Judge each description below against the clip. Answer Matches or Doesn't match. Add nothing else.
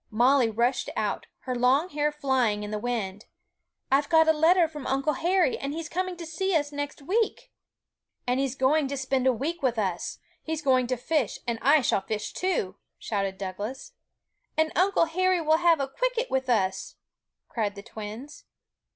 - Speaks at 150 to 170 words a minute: Doesn't match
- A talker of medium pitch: Doesn't match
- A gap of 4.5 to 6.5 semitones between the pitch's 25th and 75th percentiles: Matches